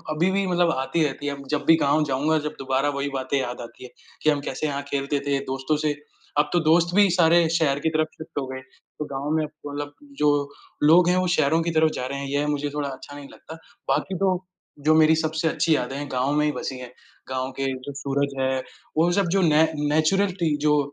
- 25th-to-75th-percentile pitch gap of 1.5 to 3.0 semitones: Yes, narrow, 2.6 semitones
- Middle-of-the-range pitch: Yes, medium, 150 Hz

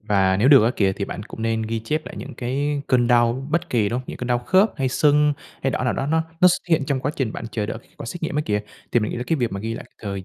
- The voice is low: Yes, low, 125 Hz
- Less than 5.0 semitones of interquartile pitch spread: Yes, average, 4.5 semitones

